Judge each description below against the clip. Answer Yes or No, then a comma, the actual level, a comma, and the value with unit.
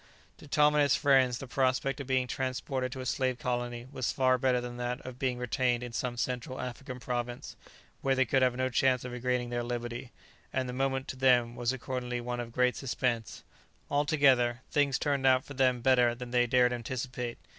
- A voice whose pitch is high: No, low, 125 Hz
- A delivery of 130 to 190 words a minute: No, average, 200 wpm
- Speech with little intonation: Yes, narrow, 1.3 semitones